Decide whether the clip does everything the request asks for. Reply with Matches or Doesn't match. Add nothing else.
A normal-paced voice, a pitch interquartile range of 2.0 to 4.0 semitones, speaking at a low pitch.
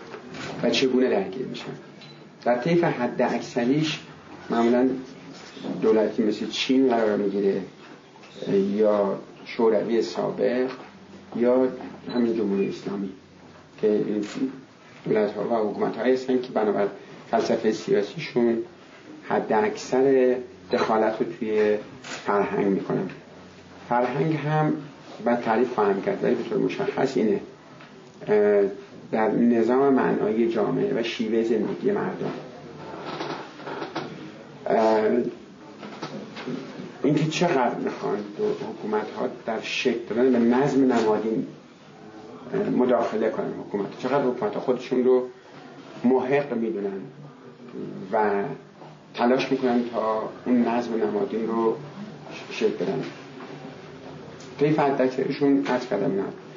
Doesn't match